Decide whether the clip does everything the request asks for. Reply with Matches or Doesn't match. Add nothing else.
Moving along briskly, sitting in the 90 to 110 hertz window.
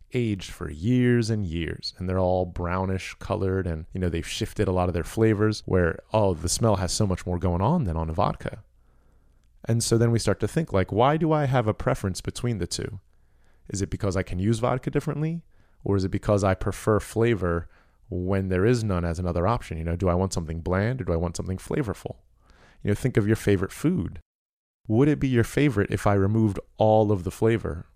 Matches